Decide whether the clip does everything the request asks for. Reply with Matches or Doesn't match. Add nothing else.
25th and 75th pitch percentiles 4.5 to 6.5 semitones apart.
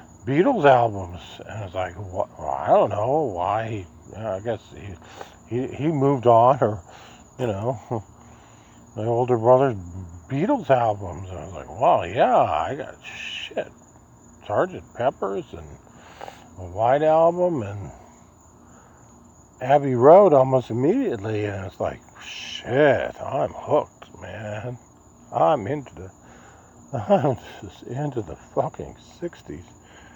Matches